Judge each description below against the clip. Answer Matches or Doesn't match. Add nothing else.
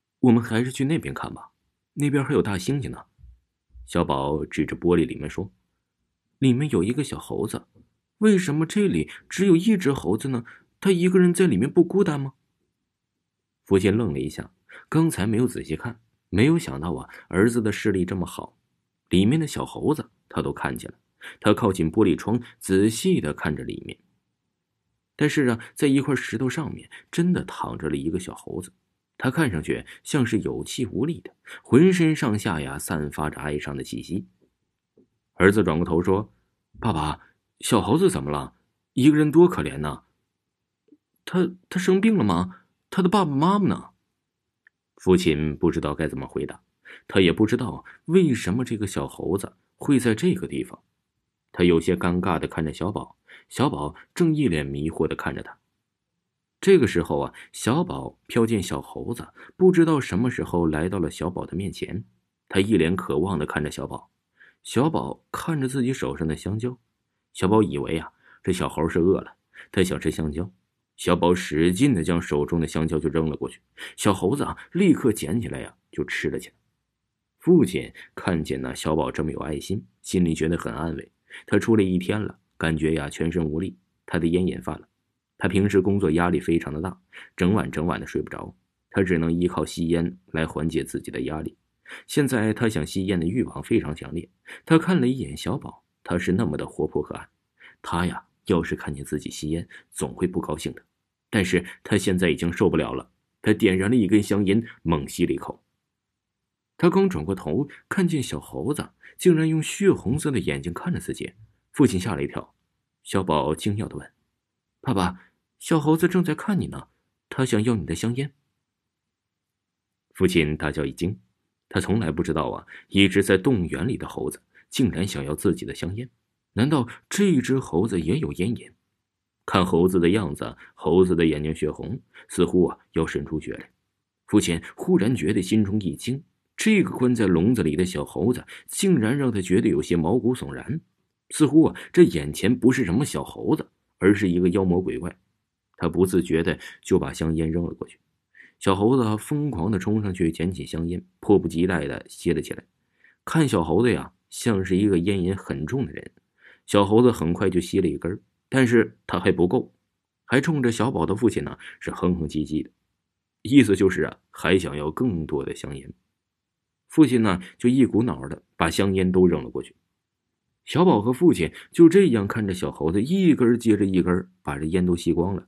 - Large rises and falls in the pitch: Matches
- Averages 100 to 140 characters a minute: Doesn't match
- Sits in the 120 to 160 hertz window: Doesn't match